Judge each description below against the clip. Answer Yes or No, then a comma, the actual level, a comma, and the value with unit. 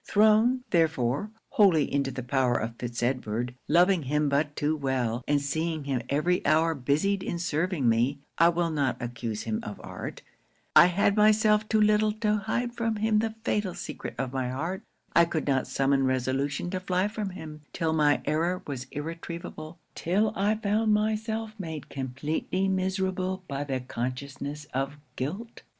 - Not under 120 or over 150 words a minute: No, average, 165 wpm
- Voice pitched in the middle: Yes, medium, 160 Hz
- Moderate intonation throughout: No, wide, 6.5 semitones